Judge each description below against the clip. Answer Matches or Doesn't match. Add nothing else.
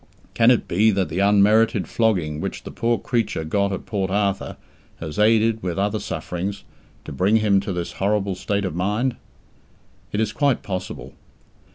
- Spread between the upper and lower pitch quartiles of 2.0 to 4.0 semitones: Matches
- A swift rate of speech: Doesn't match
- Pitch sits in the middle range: Doesn't match